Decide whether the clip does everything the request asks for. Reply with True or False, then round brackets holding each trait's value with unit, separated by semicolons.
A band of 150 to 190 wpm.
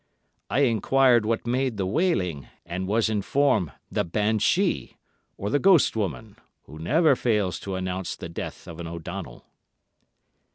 False (140 wpm)